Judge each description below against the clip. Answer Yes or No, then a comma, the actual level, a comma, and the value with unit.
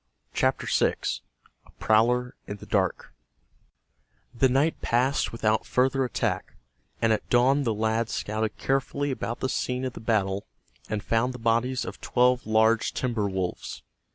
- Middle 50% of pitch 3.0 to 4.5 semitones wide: No, narrow, 2.6 semitones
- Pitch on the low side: Yes, low, 115 Hz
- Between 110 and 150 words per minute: Yes, average, 145 wpm